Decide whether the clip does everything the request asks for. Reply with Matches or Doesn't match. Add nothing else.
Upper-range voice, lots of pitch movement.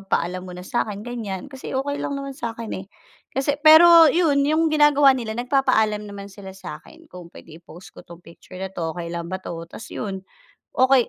Matches